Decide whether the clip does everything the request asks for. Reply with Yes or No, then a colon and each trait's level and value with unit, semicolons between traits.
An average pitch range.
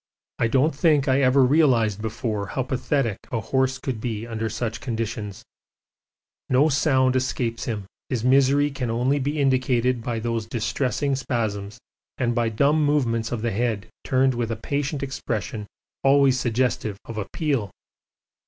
Yes: average, 3.2 semitones